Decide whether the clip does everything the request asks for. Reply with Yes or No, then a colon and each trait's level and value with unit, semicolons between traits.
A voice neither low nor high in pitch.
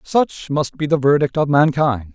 Yes: medium, 145 Hz